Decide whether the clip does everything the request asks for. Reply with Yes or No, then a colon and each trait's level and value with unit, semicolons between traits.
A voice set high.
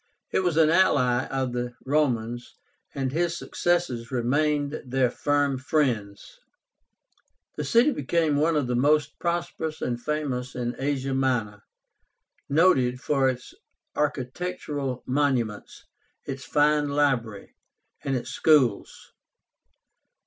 No: low, 135 Hz